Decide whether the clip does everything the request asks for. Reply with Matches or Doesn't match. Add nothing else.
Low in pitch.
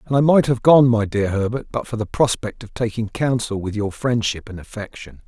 Matches